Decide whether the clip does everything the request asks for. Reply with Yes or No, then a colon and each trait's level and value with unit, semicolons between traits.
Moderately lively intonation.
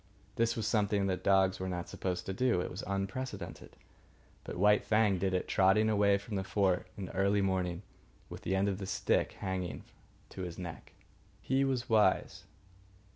No: narrow, 2.1 semitones